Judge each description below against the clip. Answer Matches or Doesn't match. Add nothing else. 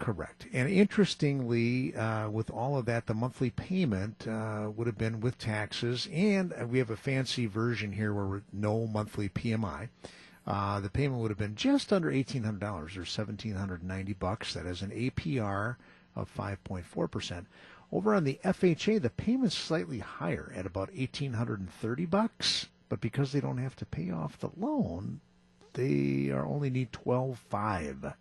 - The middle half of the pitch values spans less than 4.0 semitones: Doesn't match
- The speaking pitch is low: Matches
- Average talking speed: Matches